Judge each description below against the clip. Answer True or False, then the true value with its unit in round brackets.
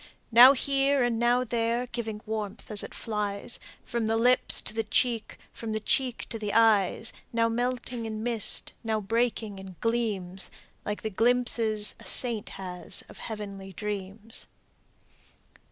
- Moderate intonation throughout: False (2.3 semitones)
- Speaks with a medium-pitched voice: False (225 Hz)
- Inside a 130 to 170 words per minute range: True (155 wpm)